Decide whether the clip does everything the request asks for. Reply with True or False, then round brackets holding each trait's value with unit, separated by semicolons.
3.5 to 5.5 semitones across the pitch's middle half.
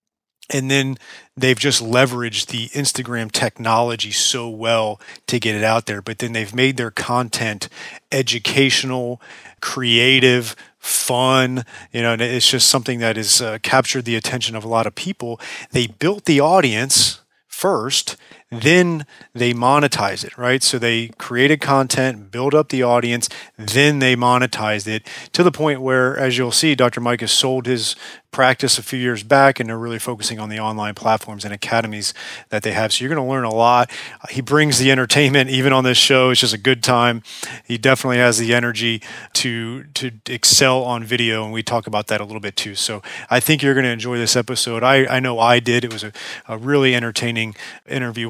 False (2.5 semitones)